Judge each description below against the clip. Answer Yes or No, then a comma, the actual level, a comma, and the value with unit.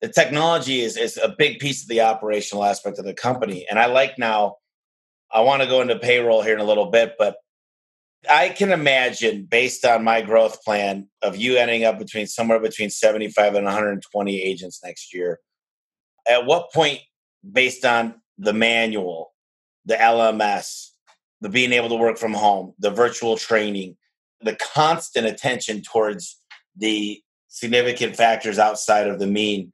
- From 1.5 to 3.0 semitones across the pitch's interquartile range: Yes, narrow, 2.6 semitones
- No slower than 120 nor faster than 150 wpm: No, average, 165 wpm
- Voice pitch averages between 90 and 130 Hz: Yes, low, 115 Hz